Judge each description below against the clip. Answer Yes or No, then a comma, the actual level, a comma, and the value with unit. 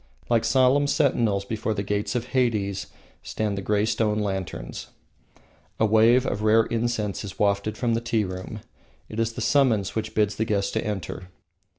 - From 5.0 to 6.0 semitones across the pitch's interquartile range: No, narrow, 2.5 semitones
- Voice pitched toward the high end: No, low, 110 Hz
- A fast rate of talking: No, average, 175 wpm